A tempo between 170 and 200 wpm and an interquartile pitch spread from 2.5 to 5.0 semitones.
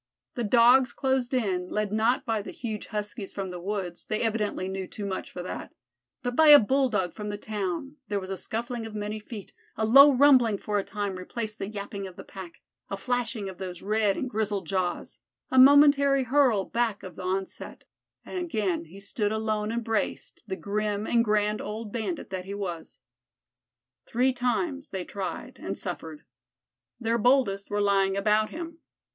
Yes: average, 180 wpm; average, 3.8 semitones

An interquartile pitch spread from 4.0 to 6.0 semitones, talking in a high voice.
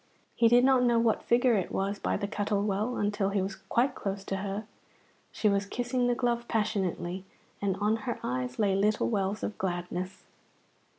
No: average, 3.3 semitones; high, 205 Hz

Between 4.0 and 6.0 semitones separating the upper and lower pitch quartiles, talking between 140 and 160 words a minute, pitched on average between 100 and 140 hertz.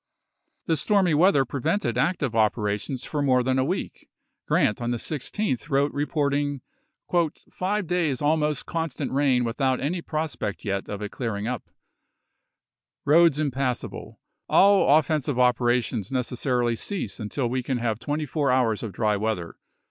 Yes: average, 4.3 semitones; average, 155 wpm; low, 135 Hz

